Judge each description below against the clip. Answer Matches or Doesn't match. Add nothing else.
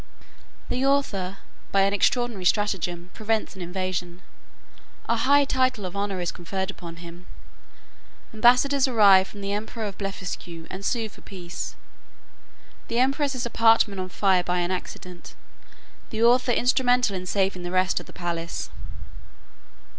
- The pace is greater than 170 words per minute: Doesn't match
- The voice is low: Doesn't match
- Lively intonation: Doesn't match